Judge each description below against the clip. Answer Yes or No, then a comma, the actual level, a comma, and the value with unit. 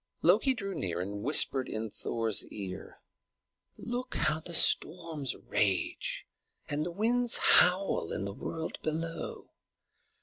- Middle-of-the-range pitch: Yes, medium, 155 Hz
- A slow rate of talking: Yes, slow, 125 wpm